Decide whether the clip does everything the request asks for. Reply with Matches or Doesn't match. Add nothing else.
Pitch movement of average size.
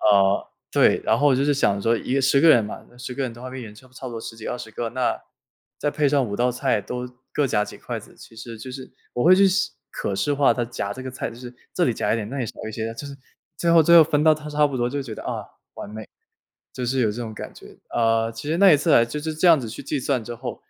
Matches